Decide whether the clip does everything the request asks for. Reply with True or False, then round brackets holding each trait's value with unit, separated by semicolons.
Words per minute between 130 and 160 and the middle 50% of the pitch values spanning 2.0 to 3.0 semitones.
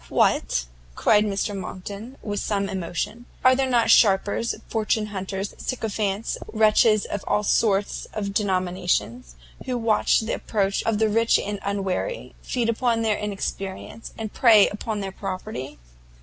True (140 wpm; 2.4 semitones)